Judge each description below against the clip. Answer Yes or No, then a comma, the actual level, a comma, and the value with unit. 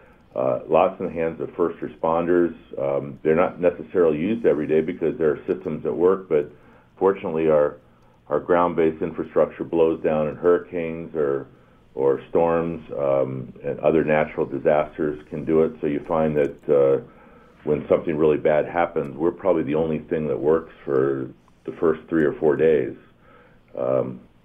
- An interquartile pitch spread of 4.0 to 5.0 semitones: No, average, 2.7 semitones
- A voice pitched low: Yes, very low, 80 Hz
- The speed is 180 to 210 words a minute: No, average, 165 wpm